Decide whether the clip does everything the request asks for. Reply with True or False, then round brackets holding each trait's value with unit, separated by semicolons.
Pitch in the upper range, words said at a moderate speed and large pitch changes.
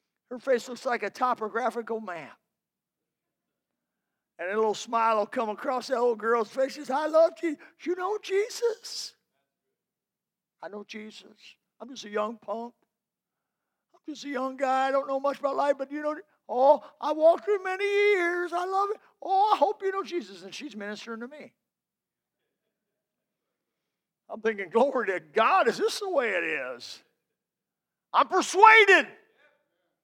True (270 Hz; 160 wpm; 7.4 semitones)